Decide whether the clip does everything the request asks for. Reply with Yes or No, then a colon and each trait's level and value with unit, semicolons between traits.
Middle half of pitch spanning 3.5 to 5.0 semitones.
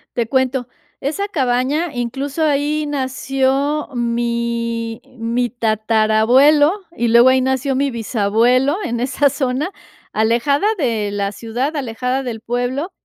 No: average, 3.1 semitones